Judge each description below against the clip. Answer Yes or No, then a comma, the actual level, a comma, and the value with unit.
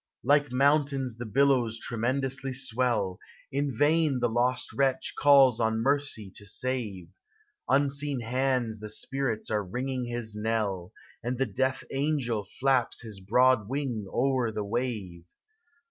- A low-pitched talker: Yes, low, 125 Hz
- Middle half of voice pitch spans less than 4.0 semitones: Yes, average, 3.5 semitones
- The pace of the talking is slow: Yes, slow, 130 wpm